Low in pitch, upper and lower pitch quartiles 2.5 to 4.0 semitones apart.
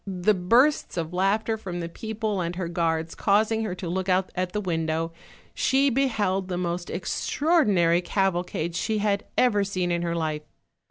No: medium, 185 Hz; average, 3.7 semitones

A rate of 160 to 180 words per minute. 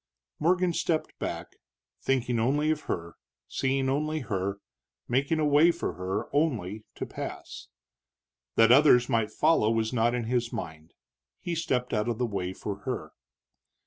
No: average, 150 wpm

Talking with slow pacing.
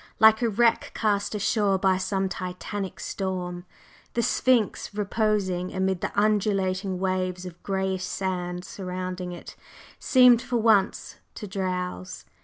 Yes: slow, 125 wpm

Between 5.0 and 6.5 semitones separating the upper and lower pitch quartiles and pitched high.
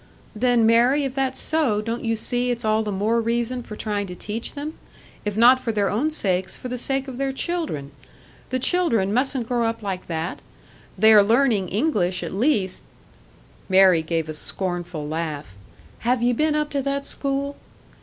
Yes: wide, 5.5 semitones; high, 230 Hz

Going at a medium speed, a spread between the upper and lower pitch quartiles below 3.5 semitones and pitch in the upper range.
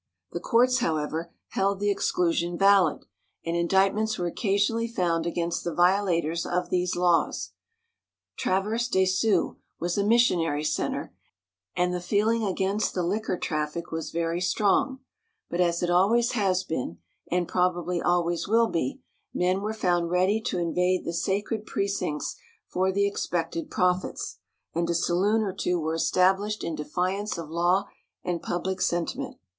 No: average, 150 wpm; average, 2.8 semitones; medium, 180 Hz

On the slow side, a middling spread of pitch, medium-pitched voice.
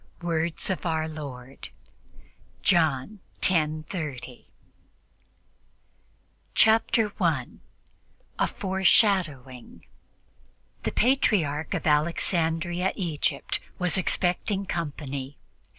Yes: slow, 70 wpm; average, 4.2 semitones; medium, 165 Hz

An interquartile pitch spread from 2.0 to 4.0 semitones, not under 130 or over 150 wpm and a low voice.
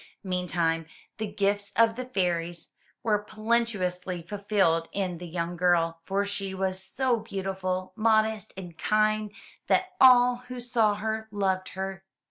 No: average, 3.2 semitones; slow, 135 wpm; high, 200 Hz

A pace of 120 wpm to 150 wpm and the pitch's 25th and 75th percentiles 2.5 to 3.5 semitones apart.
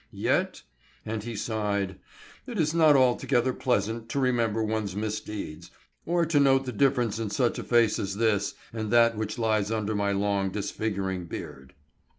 No: average, 160 wpm; average, 3.2 semitones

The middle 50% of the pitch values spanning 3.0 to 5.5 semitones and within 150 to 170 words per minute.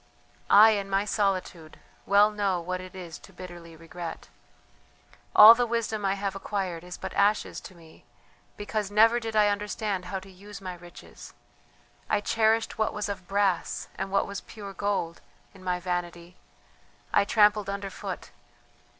No: narrow, 2.5 semitones; average, 160 wpm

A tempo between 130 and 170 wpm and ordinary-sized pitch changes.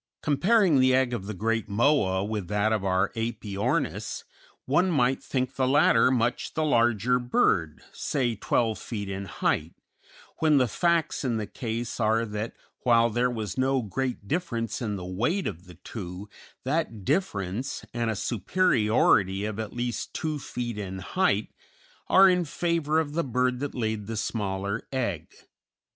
Yes: average, 160 wpm; average, 4.5 semitones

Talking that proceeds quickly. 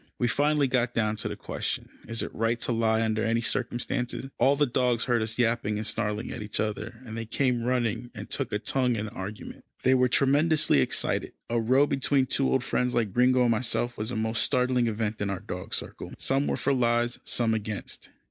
Yes: fast, 215 wpm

